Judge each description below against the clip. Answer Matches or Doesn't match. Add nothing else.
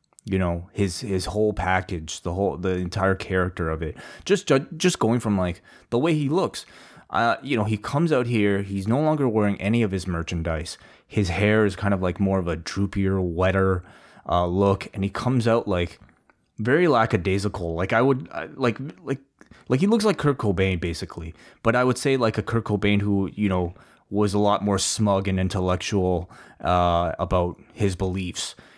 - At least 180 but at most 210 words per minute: Matches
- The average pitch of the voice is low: Matches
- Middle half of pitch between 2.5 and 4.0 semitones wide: Matches